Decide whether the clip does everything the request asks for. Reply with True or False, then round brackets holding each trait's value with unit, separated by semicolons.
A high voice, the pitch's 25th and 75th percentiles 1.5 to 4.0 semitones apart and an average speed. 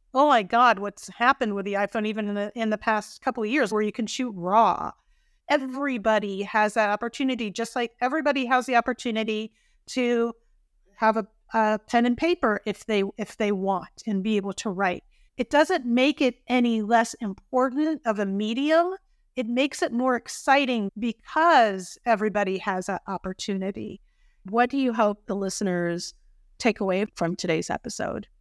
True (225 Hz; 3.7 semitones; 170 wpm)